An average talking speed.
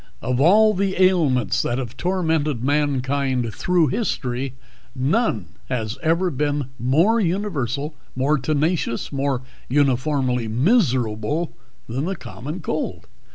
No: slow, 110 wpm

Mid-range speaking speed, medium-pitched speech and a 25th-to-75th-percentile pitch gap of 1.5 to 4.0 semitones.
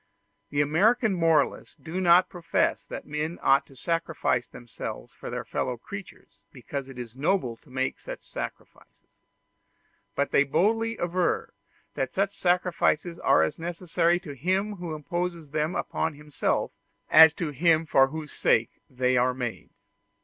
No: average, 150 wpm; medium, 160 Hz; average, 4.8 semitones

